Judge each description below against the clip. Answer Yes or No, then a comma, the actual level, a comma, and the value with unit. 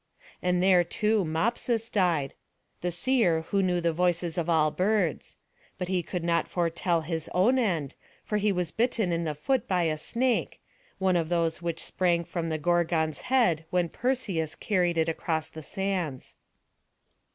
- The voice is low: No, medium, 175 Hz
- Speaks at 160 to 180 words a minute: Yes, average, 165 wpm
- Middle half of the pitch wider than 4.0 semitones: No, average, 3.0 semitones